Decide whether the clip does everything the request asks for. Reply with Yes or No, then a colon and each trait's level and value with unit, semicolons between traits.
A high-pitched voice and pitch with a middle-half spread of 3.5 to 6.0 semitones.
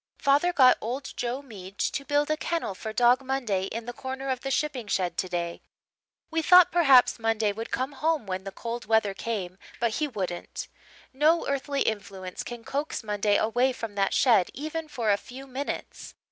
Yes: high, 240 Hz; average, 5.1 semitones